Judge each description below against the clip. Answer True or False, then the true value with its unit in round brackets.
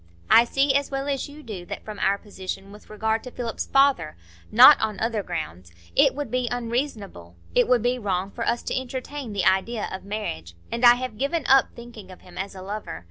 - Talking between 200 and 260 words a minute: True (205 wpm)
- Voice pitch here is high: True (220 Hz)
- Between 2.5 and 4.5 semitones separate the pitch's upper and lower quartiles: False (4.9 semitones)